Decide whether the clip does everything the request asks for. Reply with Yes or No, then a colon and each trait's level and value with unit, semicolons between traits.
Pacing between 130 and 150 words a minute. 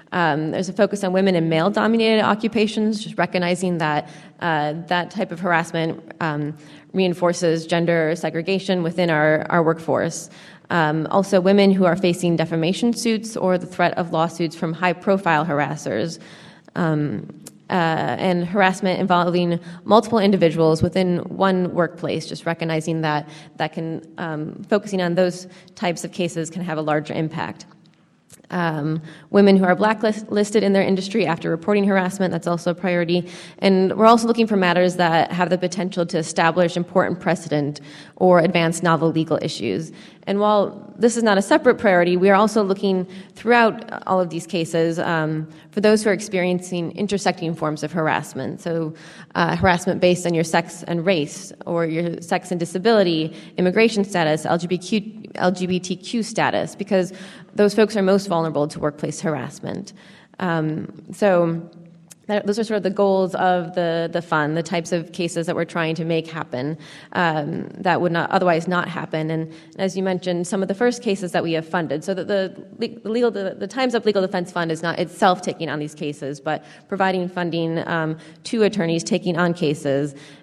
No: average, 170 wpm